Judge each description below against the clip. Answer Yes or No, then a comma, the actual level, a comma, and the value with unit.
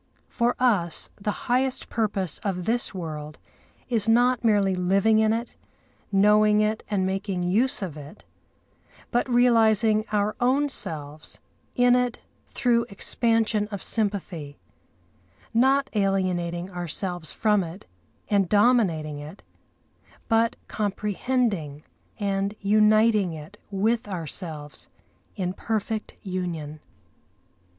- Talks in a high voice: Yes, high, 205 Hz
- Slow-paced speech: Yes, slow, 110 wpm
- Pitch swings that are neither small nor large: Yes, average, 4.1 semitones